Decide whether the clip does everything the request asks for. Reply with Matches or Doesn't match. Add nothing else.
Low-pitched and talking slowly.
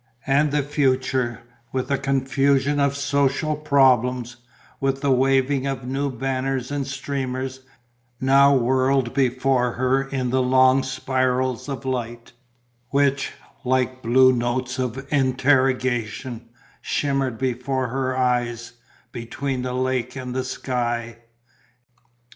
Matches